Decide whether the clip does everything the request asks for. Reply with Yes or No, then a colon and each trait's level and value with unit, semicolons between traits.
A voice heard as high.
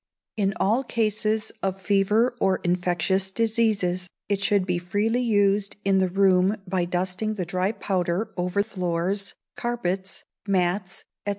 Yes: high, 195 Hz